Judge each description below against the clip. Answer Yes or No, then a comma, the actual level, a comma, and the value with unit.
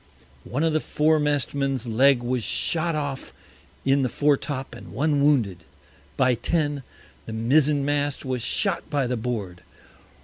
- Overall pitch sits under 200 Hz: Yes, medium, 140 Hz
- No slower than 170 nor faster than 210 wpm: No, average, 150 wpm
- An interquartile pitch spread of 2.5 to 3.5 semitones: Yes, average, 3.0 semitones